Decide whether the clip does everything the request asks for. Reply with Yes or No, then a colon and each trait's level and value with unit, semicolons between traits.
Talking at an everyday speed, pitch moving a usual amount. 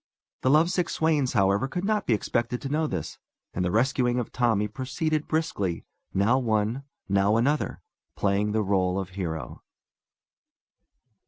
No: average, 150 wpm; wide, 6.3 semitones